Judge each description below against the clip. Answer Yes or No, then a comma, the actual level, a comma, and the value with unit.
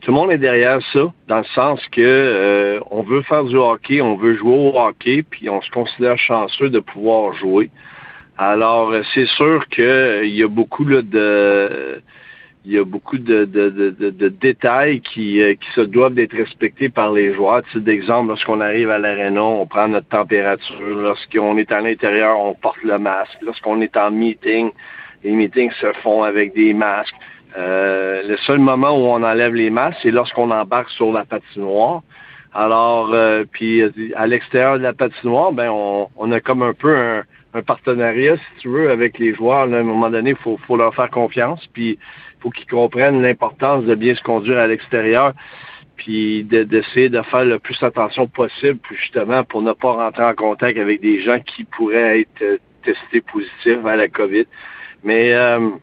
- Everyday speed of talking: Yes, average, 190 wpm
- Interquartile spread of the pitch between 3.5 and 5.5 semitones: No, average, 2.9 semitones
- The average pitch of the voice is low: Yes, low, 115 Hz